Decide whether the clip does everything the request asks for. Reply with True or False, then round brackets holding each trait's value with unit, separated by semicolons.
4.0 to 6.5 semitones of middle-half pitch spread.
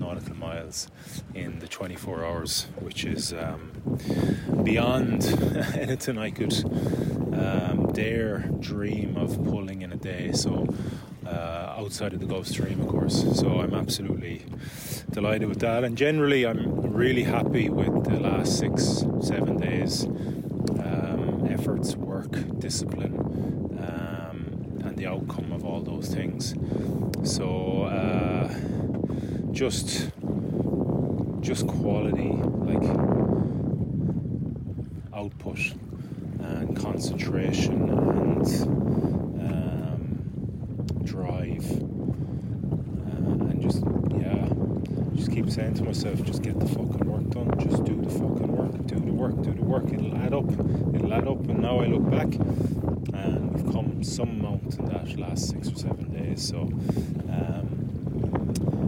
True (5.0 semitones)